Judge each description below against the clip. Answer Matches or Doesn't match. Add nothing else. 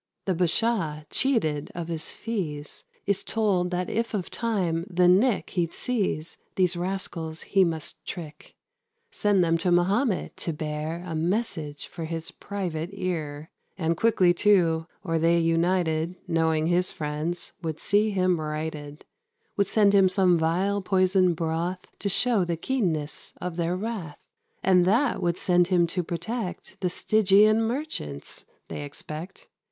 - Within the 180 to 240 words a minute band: Doesn't match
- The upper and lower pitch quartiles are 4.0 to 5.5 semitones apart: Doesn't match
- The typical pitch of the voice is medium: Matches